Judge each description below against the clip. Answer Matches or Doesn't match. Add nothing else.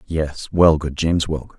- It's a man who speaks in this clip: Matches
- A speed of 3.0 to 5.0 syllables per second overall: Matches